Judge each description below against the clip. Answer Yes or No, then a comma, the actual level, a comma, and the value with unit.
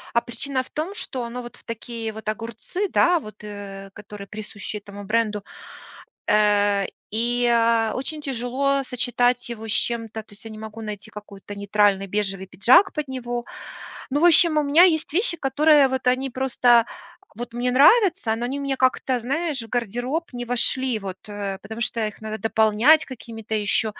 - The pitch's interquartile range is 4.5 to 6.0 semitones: No, average, 3.7 semitones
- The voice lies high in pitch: Yes, high, 235 Hz